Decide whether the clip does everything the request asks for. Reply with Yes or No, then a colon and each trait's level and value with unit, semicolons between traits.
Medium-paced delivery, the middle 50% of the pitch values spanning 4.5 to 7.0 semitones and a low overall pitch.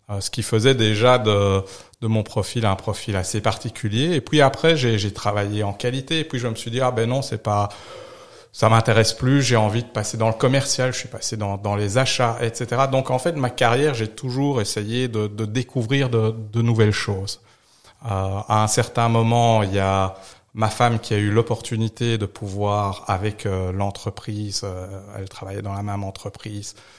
No: average, 195 wpm; average, 3.1 semitones; low, 110 Hz